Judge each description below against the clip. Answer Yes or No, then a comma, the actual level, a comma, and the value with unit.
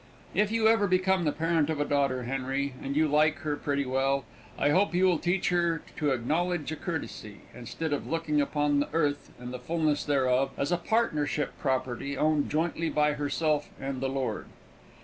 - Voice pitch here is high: No, medium, 150 Hz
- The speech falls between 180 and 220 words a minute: Yes, average, 190 wpm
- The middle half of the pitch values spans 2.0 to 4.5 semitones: Yes, average, 3.2 semitones